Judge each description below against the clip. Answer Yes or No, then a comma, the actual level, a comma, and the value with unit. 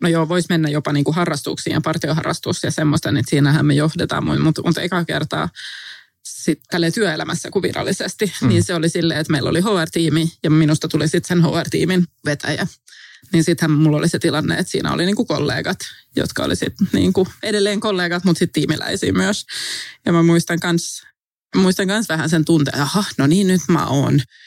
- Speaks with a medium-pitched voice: Yes, medium, 165 Hz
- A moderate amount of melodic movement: No, narrow, 2.3 semitones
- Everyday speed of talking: No, fast, 180 wpm